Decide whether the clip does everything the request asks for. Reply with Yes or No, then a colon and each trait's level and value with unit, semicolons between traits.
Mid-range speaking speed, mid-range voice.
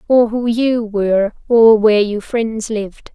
No: average, 170 wpm; high, 220 Hz